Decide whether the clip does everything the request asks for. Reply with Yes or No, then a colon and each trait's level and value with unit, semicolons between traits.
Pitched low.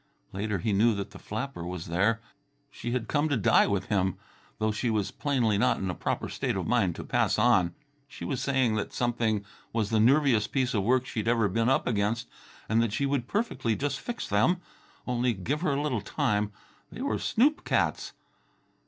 Yes: low, 115 Hz